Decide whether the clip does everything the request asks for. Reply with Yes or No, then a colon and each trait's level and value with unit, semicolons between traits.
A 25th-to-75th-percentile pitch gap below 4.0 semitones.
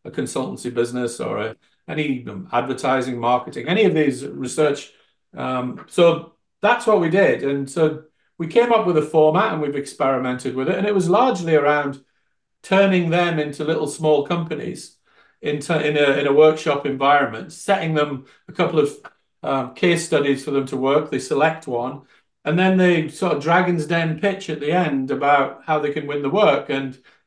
Yes: average, 3.4 semitones